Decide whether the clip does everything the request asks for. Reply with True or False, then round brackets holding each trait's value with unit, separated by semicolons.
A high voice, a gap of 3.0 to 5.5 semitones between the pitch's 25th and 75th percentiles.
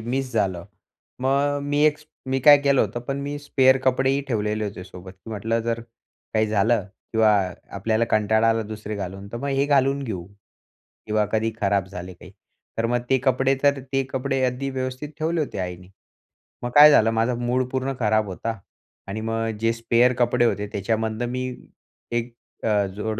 False (115 Hz; 3.6 semitones)